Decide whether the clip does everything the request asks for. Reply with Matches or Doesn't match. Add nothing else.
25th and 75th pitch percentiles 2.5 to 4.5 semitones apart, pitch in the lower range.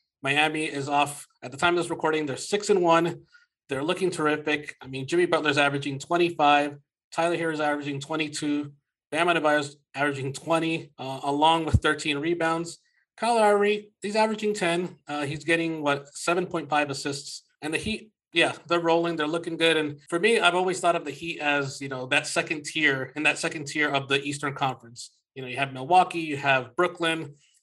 Doesn't match